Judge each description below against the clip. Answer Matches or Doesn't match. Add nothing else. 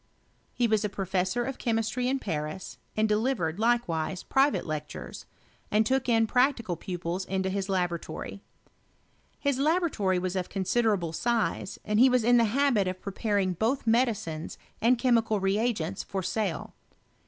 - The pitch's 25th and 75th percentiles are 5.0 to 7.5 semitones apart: Doesn't match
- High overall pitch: Matches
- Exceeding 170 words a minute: Doesn't match